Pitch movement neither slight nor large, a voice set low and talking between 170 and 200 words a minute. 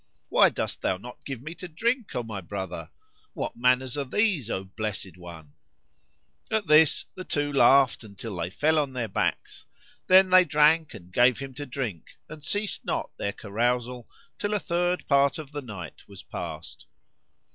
No: wide, 6.8 semitones; low, 130 Hz; average, 175 wpm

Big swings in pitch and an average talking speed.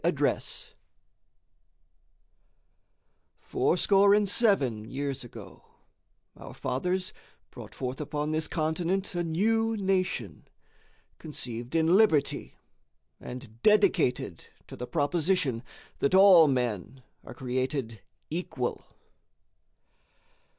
No: wide, 6.8 semitones; slow, 95 wpm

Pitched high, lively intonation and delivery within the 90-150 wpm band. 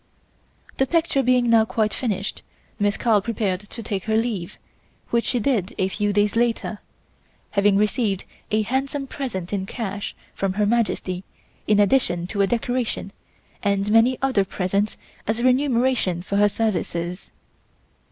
No: high, 210 Hz; average, 3.3 semitones; average, 145 wpm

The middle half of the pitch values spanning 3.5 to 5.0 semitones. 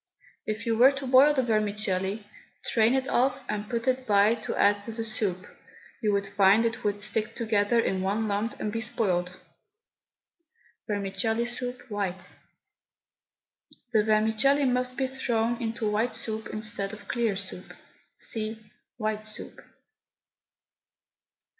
No: narrow, 2.6 semitones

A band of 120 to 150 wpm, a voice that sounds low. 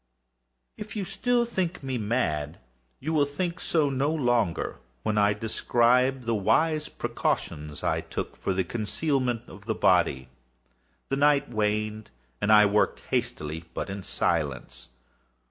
Yes: average, 140 wpm; low, 120 Hz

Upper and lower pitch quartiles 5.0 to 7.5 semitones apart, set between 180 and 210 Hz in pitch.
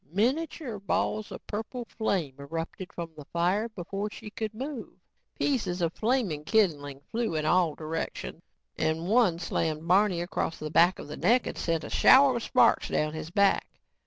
Yes: average, 5.3 semitones; medium, 185 Hz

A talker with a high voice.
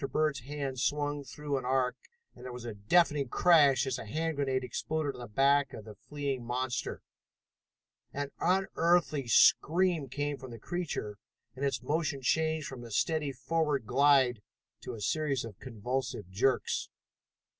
No: low, 135 Hz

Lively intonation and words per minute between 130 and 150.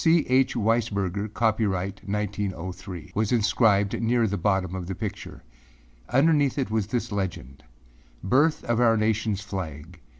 No: average, 3.5 semitones; slow, 135 wpm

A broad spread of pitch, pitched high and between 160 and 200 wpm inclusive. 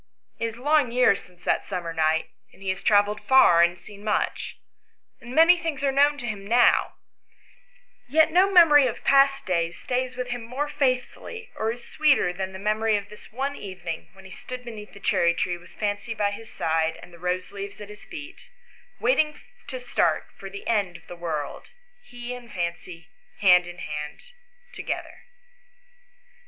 Yes: wide, 6.6 semitones; high, 215 Hz; average, 185 wpm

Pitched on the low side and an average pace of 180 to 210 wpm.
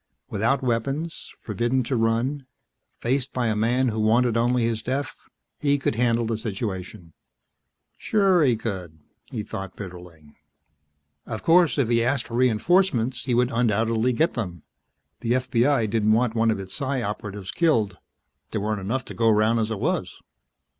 No: low, 115 Hz; average, 160 wpm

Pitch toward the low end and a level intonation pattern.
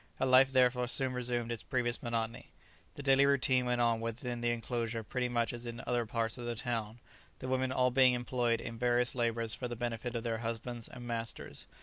Yes: low, 120 Hz; narrow, 1.4 semitones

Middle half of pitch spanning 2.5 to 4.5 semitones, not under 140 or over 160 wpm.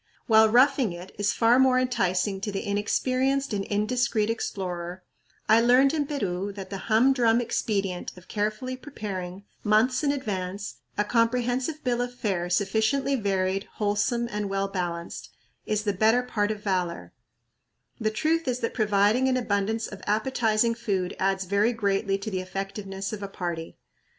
Yes: average, 3.9 semitones; average, 155 wpm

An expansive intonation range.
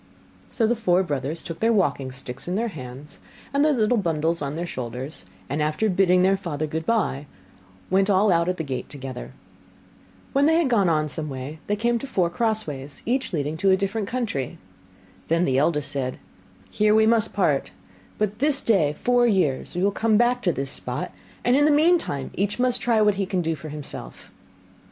Yes: wide, 7.0 semitones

